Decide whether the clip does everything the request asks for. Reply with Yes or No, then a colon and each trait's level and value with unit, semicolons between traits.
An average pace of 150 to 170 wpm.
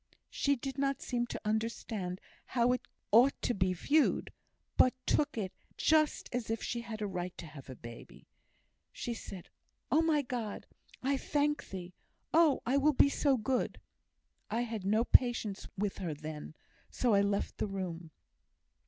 Yes: average, 165 wpm